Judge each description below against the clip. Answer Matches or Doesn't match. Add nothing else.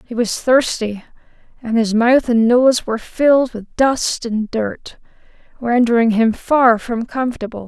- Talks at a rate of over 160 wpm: Doesn't match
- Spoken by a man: Doesn't match